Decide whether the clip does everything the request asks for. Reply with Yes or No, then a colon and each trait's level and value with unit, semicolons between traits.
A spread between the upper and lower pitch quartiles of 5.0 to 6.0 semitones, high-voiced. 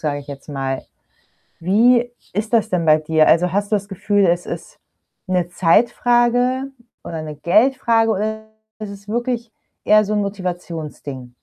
Yes: average, 5.3 semitones; high, 200 Hz